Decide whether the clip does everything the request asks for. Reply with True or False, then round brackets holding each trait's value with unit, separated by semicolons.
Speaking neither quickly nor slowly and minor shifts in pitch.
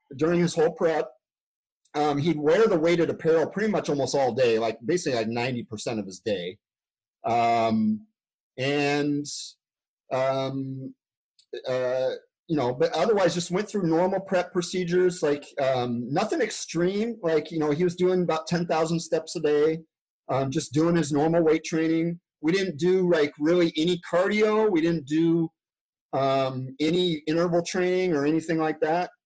False (160 wpm; 3.6 semitones)